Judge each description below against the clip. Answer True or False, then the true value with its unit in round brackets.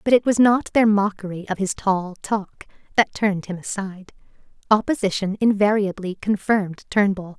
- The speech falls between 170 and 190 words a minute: False (145 wpm)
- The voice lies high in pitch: True (200 Hz)